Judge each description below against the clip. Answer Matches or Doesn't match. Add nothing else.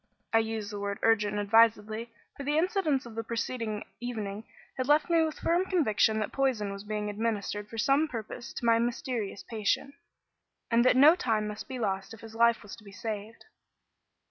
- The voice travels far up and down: Doesn't match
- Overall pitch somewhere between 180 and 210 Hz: Doesn't match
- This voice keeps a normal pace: Matches